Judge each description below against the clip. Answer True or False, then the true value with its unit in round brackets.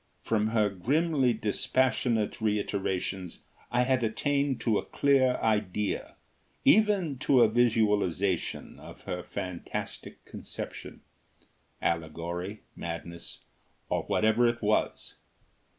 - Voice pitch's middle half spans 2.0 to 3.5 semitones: False (4.7 semitones)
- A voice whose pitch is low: True (110 Hz)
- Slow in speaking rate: True (100 wpm)